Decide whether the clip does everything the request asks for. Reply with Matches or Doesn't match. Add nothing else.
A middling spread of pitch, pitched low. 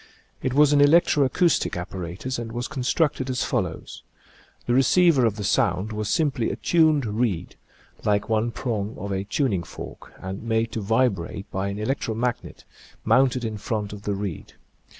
Matches